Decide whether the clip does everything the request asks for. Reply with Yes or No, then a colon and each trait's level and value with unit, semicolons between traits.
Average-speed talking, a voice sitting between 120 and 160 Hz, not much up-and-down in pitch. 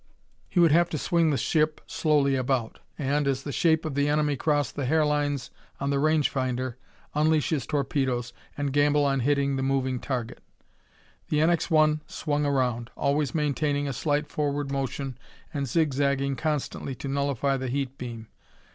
Yes: average, 170 wpm; medium, 140 Hz; narrow, 2.0 semitones